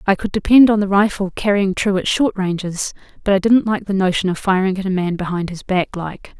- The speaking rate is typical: No, fast, 245 wpm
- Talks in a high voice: Yes, high, 195 Hz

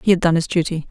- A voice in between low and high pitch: Yes, medium, 170 Hz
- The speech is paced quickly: Yes, fast, 330 wpm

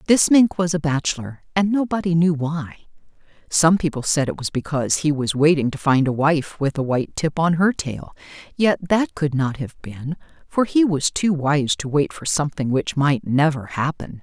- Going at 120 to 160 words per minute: No, average, 200 wpm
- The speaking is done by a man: No, female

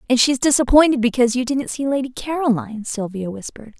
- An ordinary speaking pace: Yes, average, 175 wpm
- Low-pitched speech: No, very high, 250 Hz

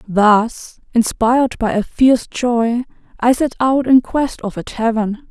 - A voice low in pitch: No, high, 240 Hz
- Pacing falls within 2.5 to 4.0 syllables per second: Yes, 3.9 syllables/s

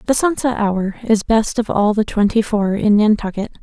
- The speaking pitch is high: Yes, high, 215 Hz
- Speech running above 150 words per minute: Yes, average, 200 wpm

